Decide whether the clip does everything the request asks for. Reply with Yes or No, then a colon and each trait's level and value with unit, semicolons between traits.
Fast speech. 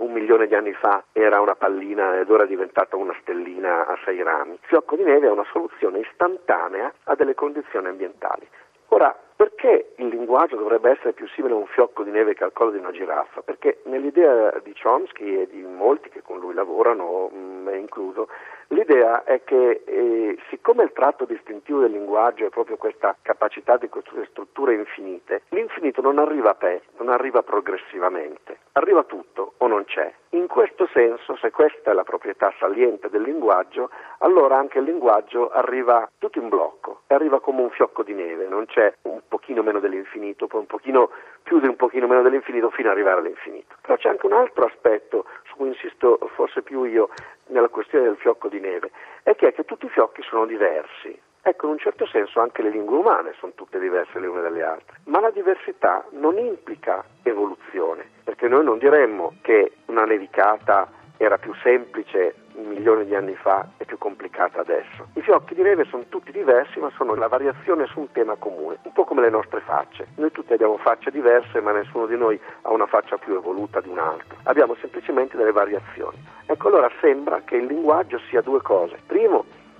Yes: fast, 190 wpm